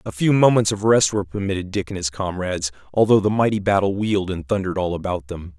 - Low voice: Yes, very low, 95 Hz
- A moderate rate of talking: No, fast, 225 wpm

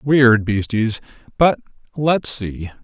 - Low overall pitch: Yes, low, 120 Hz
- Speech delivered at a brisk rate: No, slow, 85 wpm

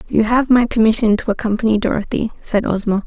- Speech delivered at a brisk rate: No, average, 175 wpm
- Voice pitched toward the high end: Yes, high, 220 Hz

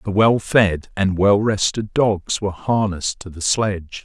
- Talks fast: No, average, 180 wpm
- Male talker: Yes, male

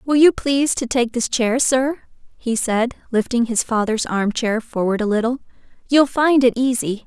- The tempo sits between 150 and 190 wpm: Yes, average, 185 wpm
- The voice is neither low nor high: No, high, 240 Hz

